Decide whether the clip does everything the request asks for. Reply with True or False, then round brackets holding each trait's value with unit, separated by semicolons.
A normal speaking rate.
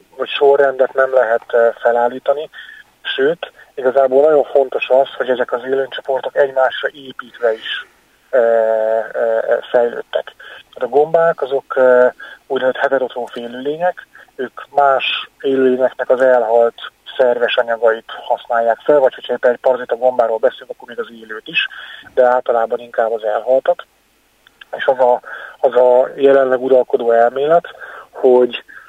True (125 wpm)